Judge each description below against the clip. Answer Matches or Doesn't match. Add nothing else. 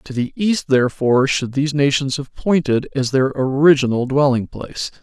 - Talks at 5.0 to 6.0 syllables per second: Matches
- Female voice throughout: Doesn't match